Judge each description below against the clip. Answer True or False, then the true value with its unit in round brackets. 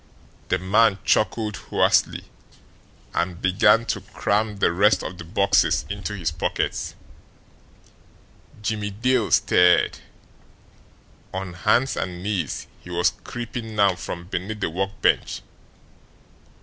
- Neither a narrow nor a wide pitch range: True (3.2 semitones)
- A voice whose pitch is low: True (100 Hz)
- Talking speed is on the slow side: True (110 wpm)